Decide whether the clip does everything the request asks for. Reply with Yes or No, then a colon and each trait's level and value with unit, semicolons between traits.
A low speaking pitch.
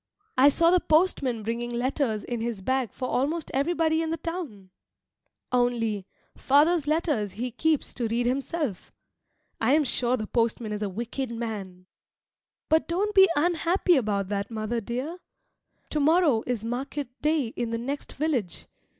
No: very high, 255 Hz